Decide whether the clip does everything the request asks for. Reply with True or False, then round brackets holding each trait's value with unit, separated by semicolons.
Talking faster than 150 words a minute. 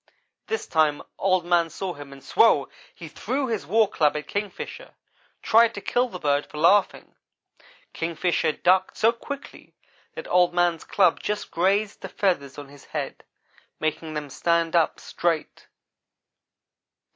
False (145 wpm)